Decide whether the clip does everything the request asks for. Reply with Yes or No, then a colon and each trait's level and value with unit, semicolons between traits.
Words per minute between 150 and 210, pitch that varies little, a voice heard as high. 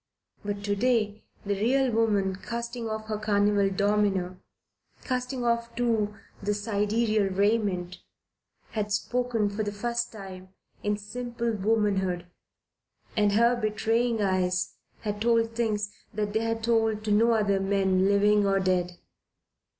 No: slow, 135 wpm; narrow, 2.2 semitones; high, 210 Hz